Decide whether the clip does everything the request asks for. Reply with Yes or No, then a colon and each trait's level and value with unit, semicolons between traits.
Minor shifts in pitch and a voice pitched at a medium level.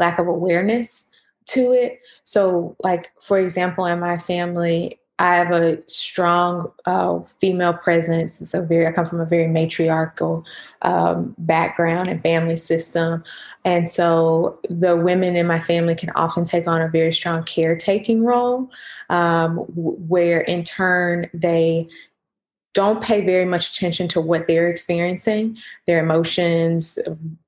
Yes: narrow, 1.5 semitones; medium, 170 Hz